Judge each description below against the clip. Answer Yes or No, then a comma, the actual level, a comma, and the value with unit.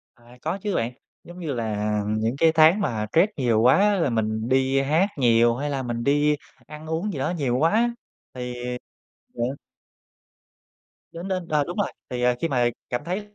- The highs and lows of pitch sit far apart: Yes, wide, 5.7 semitones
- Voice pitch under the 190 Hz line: Yes, medium, 140 Hz